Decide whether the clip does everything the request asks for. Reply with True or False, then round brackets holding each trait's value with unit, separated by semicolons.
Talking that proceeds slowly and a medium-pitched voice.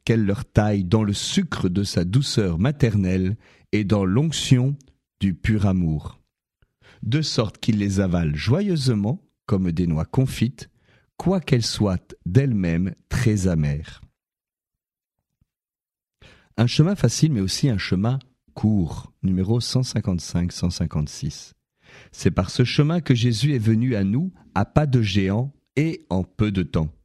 False (135 wpm; 110 Hz)